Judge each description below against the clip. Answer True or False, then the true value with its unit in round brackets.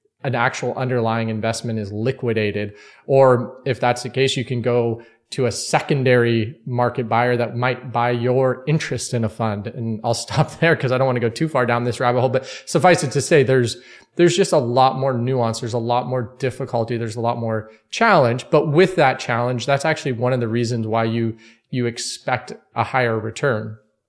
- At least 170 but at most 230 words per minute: True (205 wpm)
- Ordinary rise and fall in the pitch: False (2.2 semitones)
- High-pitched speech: False (120 Hz)